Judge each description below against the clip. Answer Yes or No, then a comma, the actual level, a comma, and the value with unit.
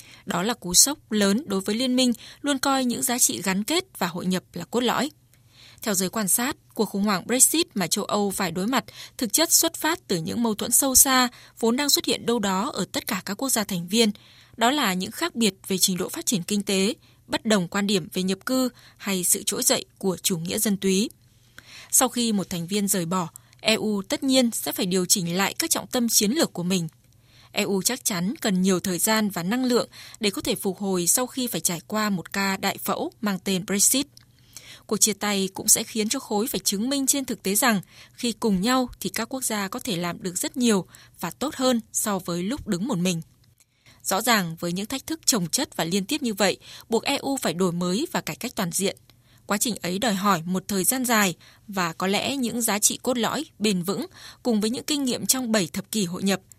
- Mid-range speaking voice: No, high, 210 Hz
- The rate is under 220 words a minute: No, average, 240 wpm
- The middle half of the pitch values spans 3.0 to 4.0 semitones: No, average, 4.6 semitones